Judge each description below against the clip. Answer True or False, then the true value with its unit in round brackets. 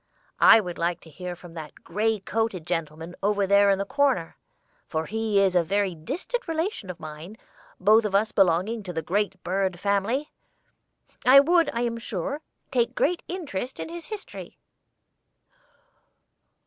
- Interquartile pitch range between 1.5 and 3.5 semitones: False (5.0 semitones)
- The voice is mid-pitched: False (200 Hz)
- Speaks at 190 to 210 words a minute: False (160 wpm)